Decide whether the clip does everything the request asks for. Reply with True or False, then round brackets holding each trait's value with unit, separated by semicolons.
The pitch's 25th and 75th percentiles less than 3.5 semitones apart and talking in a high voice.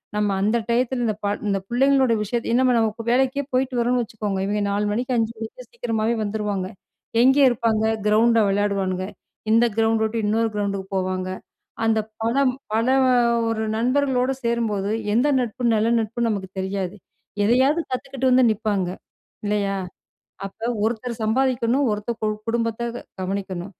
True (3.0 semitones; 225 Hz)